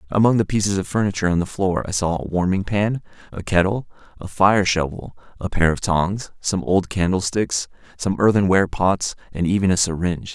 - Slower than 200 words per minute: Yes, average, 190 wpm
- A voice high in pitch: No, very low, 95 Hz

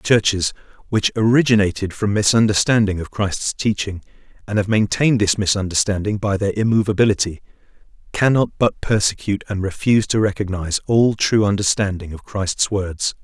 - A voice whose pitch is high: No, low, 105 Hz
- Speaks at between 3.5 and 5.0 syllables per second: No, 5.5 syllables/s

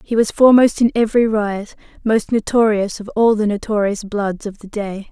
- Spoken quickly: No, average, 190 wpm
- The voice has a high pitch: Yes, high, 215 Hz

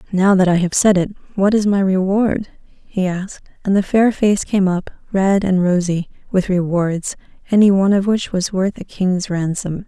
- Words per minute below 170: No, average, 190 wpm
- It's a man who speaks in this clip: No, female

